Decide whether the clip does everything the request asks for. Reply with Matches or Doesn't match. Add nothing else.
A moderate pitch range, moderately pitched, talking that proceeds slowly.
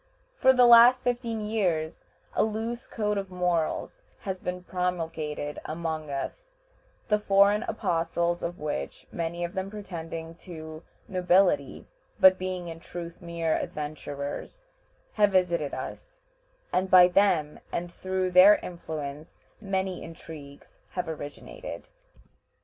Matches